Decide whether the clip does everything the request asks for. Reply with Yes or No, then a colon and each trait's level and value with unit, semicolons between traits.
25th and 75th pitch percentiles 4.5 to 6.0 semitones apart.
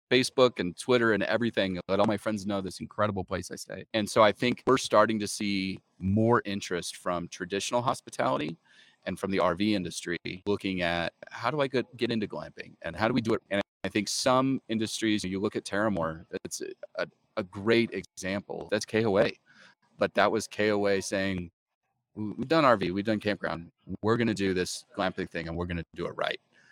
No: average, 3.3 semitones